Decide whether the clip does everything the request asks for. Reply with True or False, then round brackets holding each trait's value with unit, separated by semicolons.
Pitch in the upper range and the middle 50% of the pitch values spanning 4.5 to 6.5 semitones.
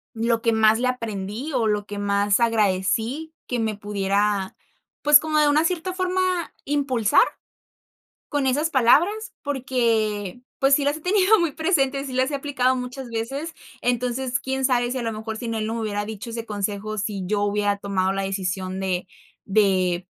True (230 Hz; 5.1 semitones)